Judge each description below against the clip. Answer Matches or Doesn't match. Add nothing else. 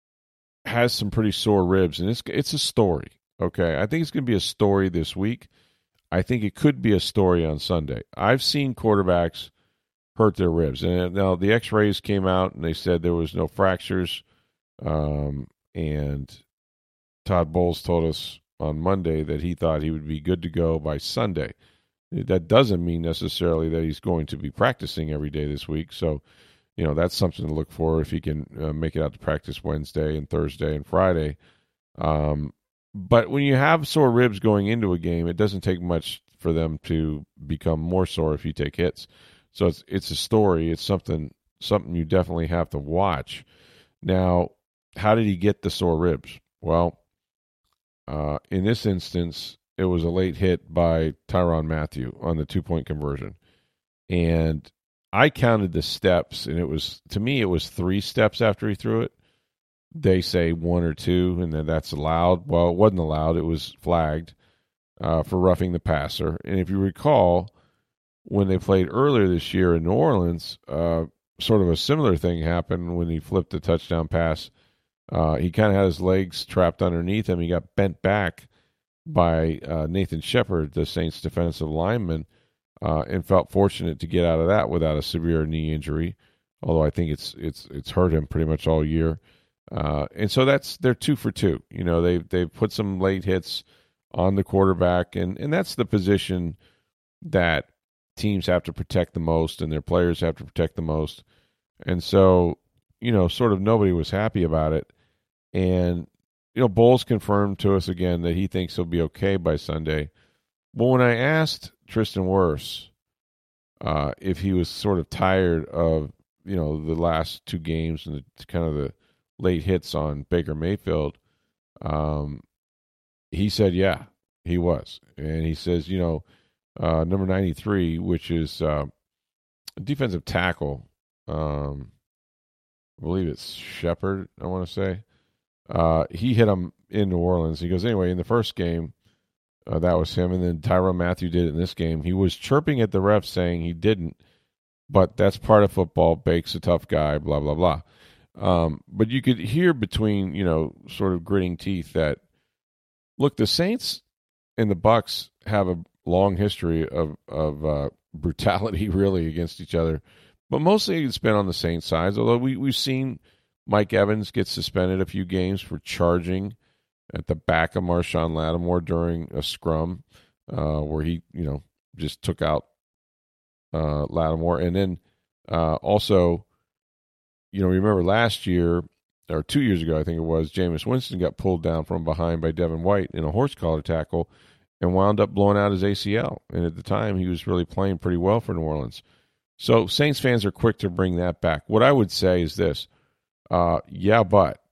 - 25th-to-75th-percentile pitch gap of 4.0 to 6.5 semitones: Doesn't match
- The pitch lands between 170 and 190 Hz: Doesn't match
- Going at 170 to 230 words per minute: Matches